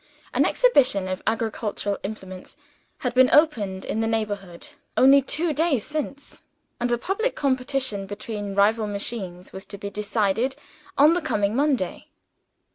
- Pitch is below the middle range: No, high, 225 Hz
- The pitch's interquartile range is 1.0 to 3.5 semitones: No, average, 5.3 semitones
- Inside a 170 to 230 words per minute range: No, average, 140 wpm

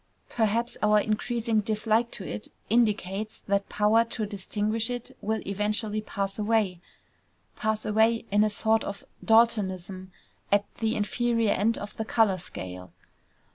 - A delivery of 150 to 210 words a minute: No, slow, 135 wpm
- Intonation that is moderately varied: No, narrow, 2.0 semitones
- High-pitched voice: Yes, high, 215 Hz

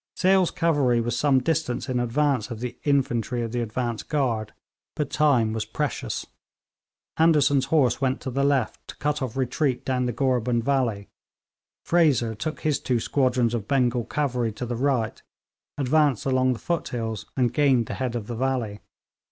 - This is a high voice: No, low, 130 Hz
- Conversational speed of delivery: Yes, average, 170 wpm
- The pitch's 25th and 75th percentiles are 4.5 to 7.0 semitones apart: No, average, 3.2 semitones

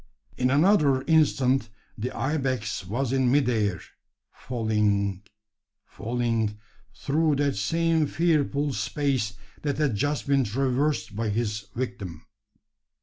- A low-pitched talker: Yes, low, 130 Hz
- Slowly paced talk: Yes, slow, 115 wpm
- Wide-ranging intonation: No, average, 5.0 semitones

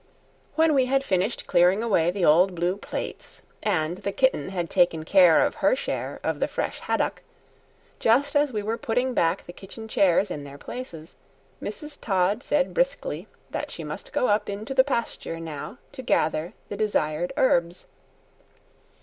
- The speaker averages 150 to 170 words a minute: Yes, average, 165 wpm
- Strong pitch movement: Yes, wide, 6.7 semitones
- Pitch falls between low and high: No, high, 200 Hz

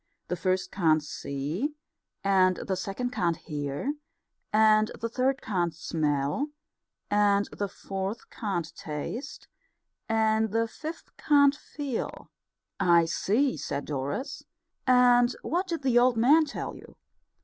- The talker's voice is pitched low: No, high, 210 Hz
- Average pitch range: No, wide, 6.9 semitones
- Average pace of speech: No, slow, 125 wpm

